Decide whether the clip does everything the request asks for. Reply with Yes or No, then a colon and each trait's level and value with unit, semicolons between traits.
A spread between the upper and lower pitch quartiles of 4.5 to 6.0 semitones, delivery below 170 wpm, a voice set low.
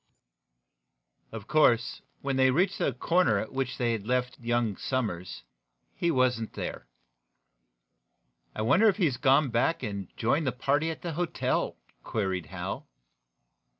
Yes: average, 5.0 semitones; average, 150 wpm; low, 125 Hz